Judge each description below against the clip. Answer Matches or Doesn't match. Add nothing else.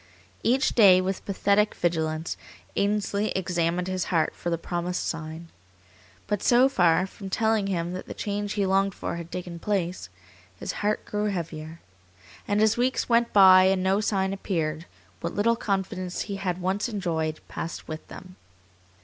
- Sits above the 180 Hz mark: Matches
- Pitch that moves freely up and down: Doesn't match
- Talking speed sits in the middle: Matches